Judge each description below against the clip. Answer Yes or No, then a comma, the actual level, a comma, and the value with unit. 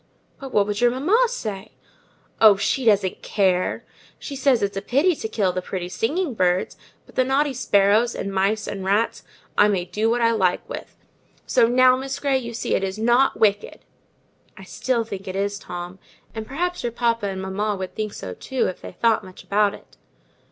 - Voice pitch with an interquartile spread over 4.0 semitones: Yes, average, 4.5 semitones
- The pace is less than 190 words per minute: No, average, 200 wpm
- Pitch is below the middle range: No, high, 215 Hz